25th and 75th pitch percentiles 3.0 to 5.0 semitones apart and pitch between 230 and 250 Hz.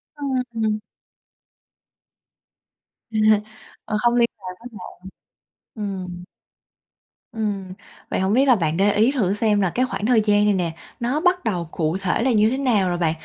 No: average, 4.3 semitones; high, 210 Hz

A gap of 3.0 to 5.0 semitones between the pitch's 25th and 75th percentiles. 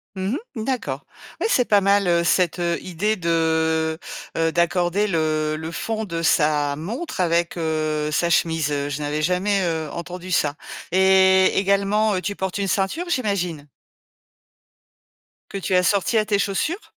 Yes: average, 3.7 semitones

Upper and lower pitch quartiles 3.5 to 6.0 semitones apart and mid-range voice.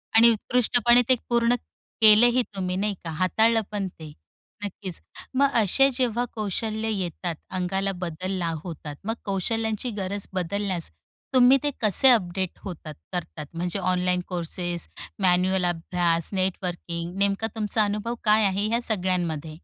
No: average, 3.8 semitones; high, 195 Hz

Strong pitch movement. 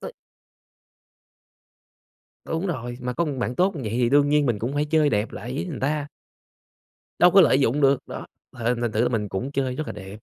No: average, 3.9 semitones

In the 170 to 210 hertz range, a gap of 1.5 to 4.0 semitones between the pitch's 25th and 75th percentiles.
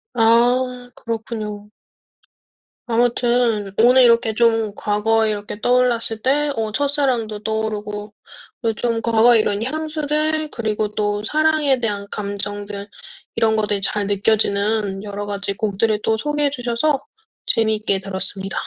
No: high, 220 Hz; average, 2.9 semitones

